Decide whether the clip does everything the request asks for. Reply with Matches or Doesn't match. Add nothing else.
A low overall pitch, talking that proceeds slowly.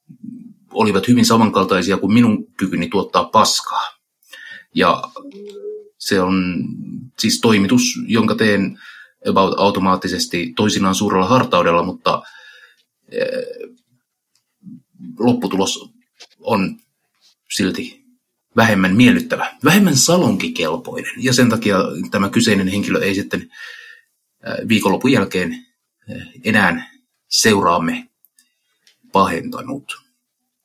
Doesn't match